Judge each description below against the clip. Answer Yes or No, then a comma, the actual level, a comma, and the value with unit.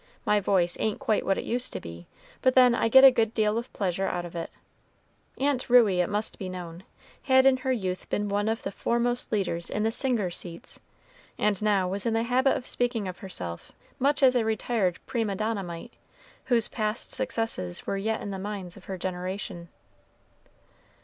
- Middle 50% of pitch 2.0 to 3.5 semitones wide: No, average, 4.4 semitones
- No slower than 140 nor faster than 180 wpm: No, average, 195 wpm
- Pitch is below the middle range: No, high, 210 Hz